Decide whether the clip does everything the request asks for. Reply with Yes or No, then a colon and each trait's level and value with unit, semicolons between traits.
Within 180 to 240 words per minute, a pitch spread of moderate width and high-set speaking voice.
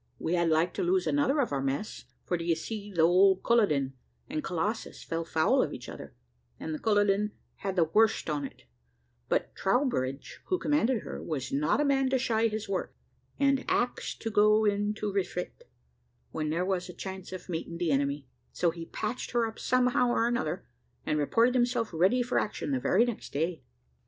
No: average, 190 wpm; wide, 6.4 semitones; high, 200 Hz